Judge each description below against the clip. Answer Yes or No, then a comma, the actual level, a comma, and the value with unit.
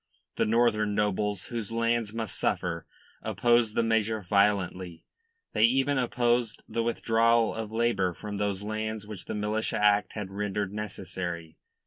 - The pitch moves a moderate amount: No, narrow, 2.2 semitones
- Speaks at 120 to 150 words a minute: Yes, average, 140 wpm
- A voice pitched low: Yes, low, 105 Hz